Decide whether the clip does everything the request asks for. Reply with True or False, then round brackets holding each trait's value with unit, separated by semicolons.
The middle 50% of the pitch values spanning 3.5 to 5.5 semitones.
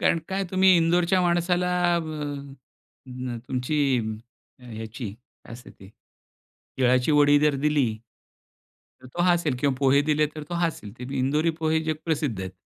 True (5.2 semitones)